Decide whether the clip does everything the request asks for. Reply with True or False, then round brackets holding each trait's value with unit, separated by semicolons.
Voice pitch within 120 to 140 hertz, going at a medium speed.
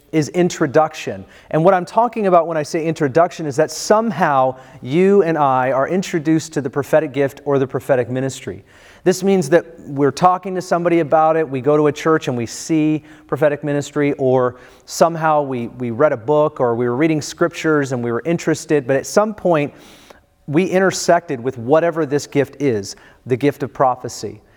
False (150 Hz; 190 wpm)